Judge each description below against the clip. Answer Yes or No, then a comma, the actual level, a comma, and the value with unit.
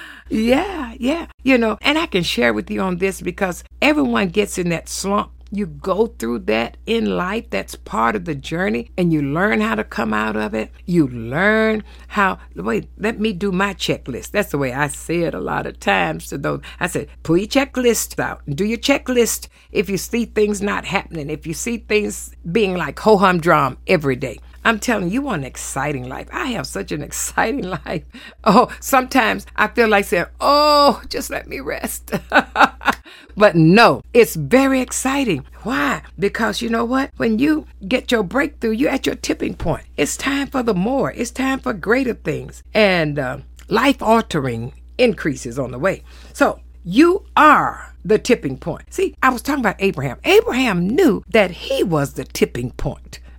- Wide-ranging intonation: Yes, wide, 7.1 semitones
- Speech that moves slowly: No, average, 190 wpm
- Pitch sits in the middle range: No, high, 210 Hz